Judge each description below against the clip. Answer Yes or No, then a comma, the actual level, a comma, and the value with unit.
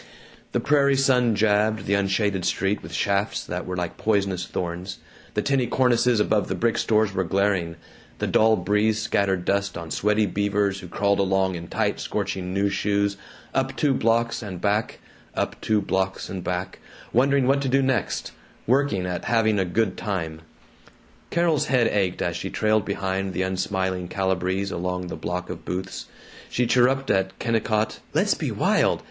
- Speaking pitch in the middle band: No, low, 100 Hz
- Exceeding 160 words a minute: Yes, average, 170 wpm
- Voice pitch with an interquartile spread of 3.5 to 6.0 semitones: No, average, 3.1 semitones